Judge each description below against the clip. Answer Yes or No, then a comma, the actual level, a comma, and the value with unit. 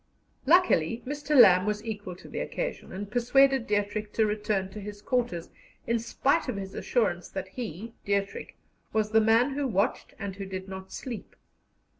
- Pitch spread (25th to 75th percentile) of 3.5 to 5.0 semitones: Yes, average, 3.9 semitones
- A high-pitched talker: Yes, high, 210 Hz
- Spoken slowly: No, average, 170 wpm